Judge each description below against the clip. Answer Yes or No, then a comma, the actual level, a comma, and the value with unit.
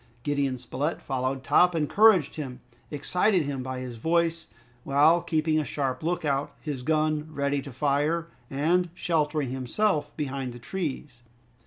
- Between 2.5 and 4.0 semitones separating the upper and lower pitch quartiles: Yes, average, 3.3 semitones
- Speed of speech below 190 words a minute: Yes, average, 145 wpm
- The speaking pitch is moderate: Yes, medium, 150 Hz